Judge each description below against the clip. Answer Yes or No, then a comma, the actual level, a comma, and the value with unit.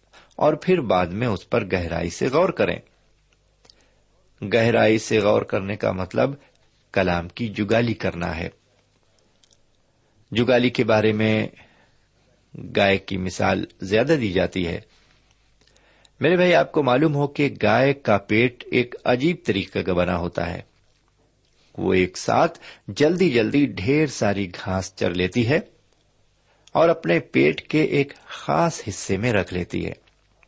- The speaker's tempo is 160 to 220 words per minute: No, average, 140 wpm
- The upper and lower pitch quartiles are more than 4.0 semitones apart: Yes, average, 4.8 semitones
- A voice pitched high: No, low, 110 Hz